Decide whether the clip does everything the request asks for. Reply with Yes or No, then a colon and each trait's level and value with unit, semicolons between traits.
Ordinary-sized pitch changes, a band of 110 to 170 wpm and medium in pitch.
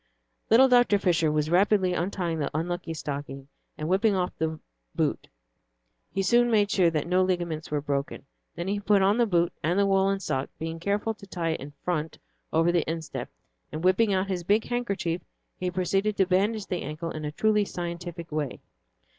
No: average, 3.7 semitones; average, 190 wpm; medium, 180 Hz